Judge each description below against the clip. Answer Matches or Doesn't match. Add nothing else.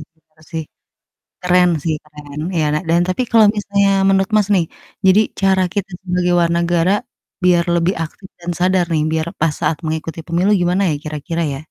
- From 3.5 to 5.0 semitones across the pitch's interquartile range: Doesn't match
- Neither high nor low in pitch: Matches